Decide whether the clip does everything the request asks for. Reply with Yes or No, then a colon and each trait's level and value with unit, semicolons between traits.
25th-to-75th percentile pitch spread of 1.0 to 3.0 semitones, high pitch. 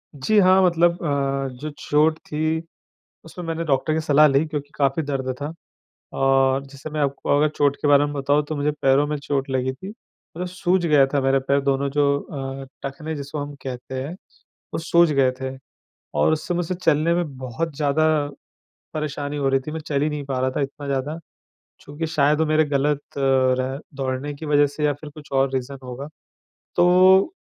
No: narrow, 2.4 semitones; medium, 145 Hz